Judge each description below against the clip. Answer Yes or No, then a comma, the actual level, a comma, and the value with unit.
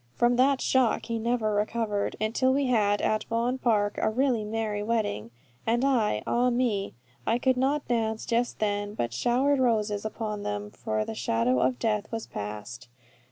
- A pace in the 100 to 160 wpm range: No, average, 175 wpm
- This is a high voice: Yes, high, 220 Hz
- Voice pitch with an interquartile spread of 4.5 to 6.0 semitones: No, average, 3.0 semitones